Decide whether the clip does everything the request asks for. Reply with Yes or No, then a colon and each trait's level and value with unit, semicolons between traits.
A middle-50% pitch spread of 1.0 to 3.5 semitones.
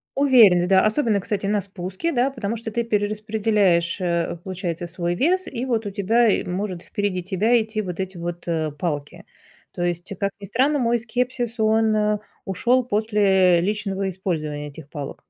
No: average, 4.1 semitones